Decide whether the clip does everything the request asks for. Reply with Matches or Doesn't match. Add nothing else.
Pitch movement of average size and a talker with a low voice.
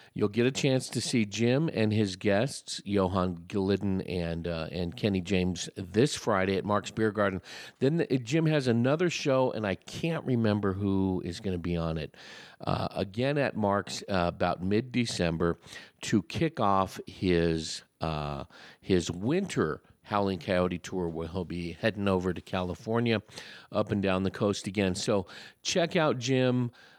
Matches